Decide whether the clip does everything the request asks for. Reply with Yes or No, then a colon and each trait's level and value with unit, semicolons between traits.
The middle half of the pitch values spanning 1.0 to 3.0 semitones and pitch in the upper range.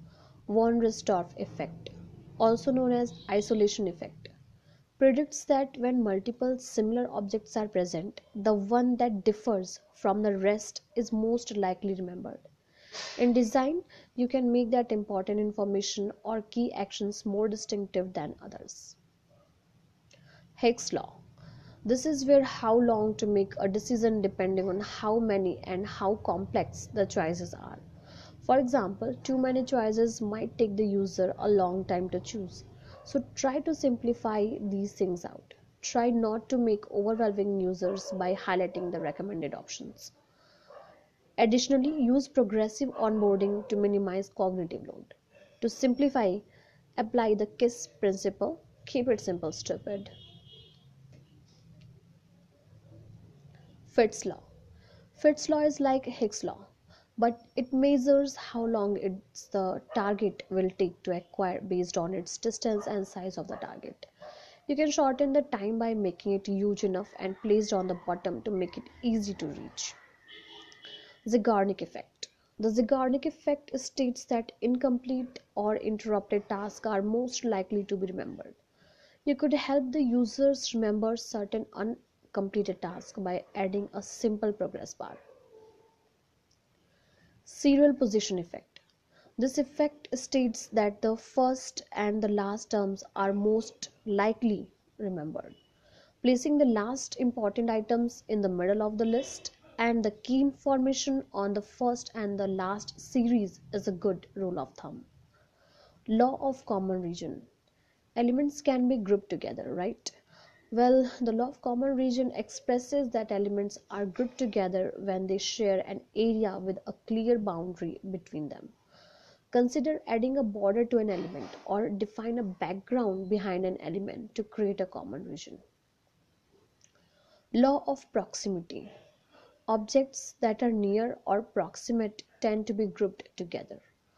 No: average, 4.0 semitones; high, 215 Hz